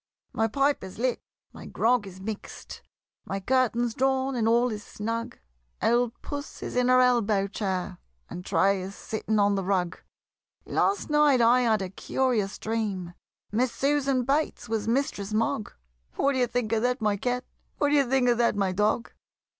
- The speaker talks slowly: No, average, 170 wpm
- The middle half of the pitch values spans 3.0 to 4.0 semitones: Yes, average, 3.7 semitones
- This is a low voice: No, high, 230 Hz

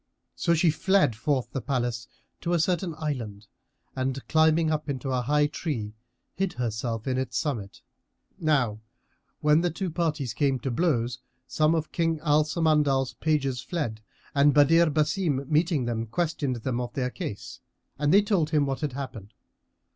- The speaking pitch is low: No, medium, 145 Hz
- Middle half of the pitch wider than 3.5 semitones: Yes, average, 4.2 semitones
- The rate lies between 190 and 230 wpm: No, average, 160 wpm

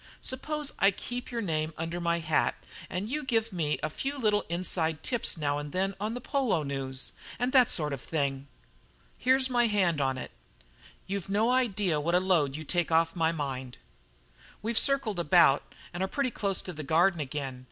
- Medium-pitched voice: Yes, medium, 175 Hz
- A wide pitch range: Yes, wide, 6.6 semitones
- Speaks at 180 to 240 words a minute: Yes, average, 185 wpm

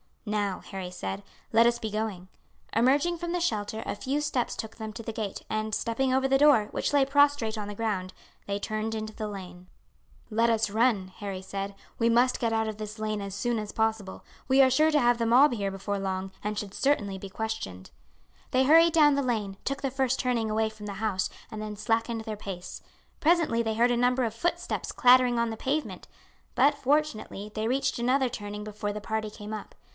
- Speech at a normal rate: No, fast, 210 wpm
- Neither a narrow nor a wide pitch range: Yes, average, 3.6 semitones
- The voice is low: No, high, 220 Hz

